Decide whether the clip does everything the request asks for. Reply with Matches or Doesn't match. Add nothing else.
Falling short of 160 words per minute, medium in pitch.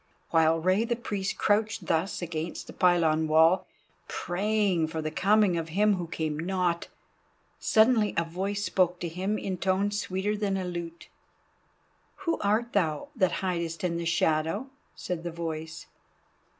Matches